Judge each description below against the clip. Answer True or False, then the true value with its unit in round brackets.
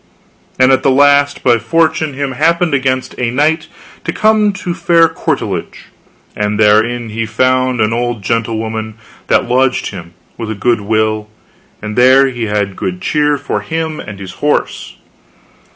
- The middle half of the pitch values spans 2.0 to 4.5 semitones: False (5.1 semitones)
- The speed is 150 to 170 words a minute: True (165 wpm)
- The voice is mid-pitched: False (125 Hz)